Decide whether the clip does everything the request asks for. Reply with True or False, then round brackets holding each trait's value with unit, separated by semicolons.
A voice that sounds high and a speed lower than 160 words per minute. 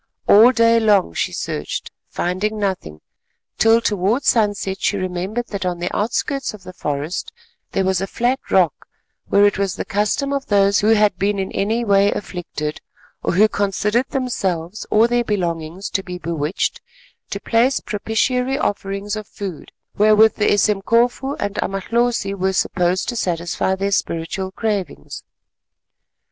True (200 Hz; 150 wpm)